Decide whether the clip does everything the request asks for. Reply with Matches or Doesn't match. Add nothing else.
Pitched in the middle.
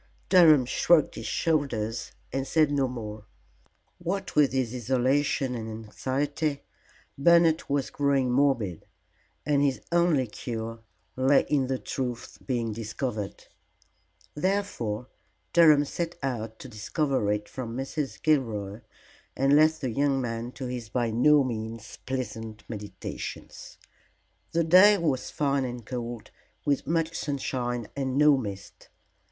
Doesn't match